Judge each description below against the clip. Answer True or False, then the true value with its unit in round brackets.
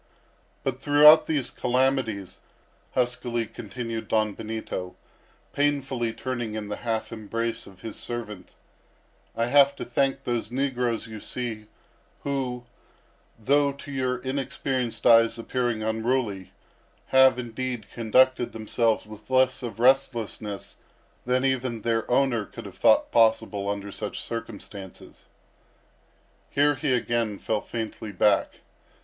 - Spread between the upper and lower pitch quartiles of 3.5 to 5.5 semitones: False (2.9 semitones)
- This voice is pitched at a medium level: False (120 Hz)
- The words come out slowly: True (120 wpm)